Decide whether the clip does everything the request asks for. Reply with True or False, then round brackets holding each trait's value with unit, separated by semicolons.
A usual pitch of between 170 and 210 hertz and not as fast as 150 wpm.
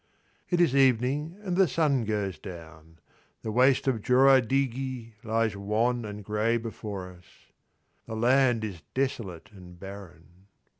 False (115 Hz; 135 wpm)